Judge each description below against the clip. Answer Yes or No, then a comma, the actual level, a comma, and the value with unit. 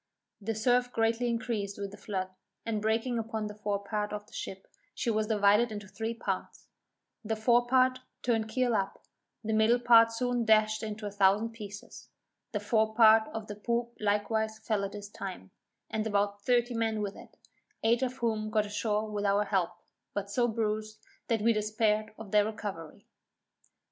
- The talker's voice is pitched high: Yes, high, 215 Hz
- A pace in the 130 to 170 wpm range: No, average, 180 wpm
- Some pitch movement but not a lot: No, narrow, 1.8 semitones